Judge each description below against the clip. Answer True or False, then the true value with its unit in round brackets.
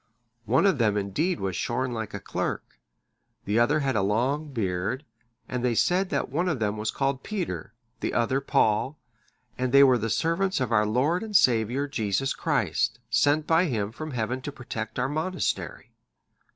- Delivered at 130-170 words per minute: False (180 wpm)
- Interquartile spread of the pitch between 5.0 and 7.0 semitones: True (5.4 semitones)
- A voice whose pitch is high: False (130 Hz)